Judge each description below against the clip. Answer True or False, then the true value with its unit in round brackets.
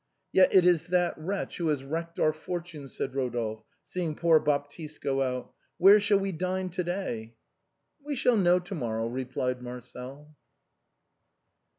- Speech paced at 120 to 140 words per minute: False (165 wpm)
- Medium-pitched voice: True (155 Hz)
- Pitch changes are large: True (5.7 semitones)